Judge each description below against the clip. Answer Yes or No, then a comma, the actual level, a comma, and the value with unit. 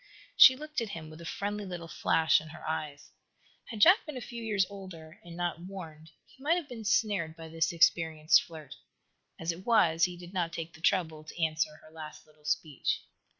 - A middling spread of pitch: Yes, average, 4.3 semitones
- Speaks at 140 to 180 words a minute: No, fast, 205 wpm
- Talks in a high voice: No, medium, 170 Hz